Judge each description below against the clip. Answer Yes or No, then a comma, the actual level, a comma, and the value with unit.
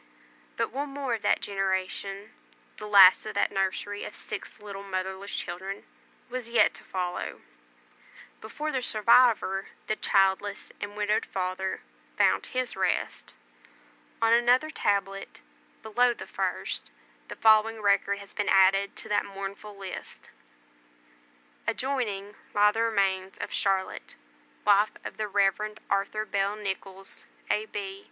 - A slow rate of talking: Yes, slow, 130 wpm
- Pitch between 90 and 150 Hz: No, high, 200 Hz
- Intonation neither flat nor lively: No, narrow, 2.0 semitones